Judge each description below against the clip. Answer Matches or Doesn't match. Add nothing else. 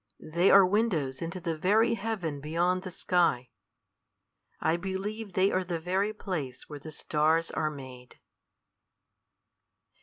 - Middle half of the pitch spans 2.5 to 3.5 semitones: Doesn't match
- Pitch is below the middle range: Doesn't match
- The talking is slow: Matches